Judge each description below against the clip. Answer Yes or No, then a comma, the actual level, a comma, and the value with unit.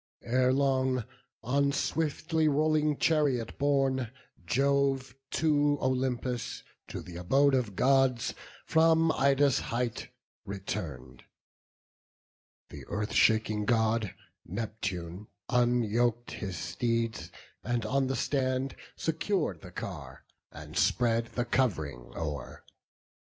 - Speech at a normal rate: No, slow, 100 wpm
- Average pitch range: Yes, average, 4.4 semitones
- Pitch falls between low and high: No, low, 125 Hz